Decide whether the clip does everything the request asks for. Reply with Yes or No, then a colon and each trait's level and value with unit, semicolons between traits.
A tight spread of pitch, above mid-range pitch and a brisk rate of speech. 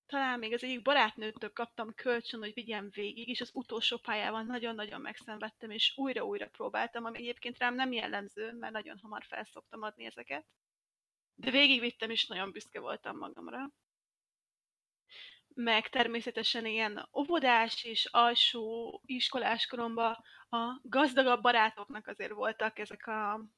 No: narrow, 2.1 semitones; high, 235 Hz; average, 130 wpm